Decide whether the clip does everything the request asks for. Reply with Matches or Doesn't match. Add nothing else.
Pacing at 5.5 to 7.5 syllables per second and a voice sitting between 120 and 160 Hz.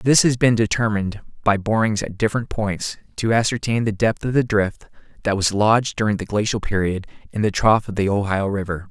Doesn't match